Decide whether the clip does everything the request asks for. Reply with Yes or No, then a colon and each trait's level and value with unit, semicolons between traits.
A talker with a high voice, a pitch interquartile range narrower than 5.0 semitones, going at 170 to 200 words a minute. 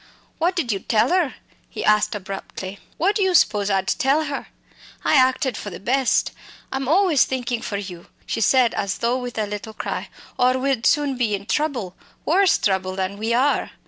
No: high, 245 Hz; wide, 5.6 semitones; average, 190 wpm